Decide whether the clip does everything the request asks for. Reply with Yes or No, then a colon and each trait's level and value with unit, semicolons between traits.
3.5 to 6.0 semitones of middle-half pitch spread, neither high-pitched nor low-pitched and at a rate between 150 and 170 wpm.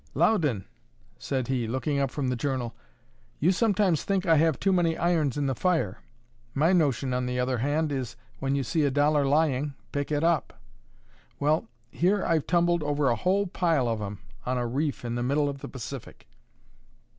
No: average, 4.3 semitones; medium, 145 Hz; average, 190 wpm